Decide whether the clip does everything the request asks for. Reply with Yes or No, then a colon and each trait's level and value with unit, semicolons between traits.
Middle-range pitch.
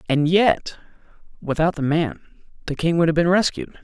Yes: medium, 165 Hz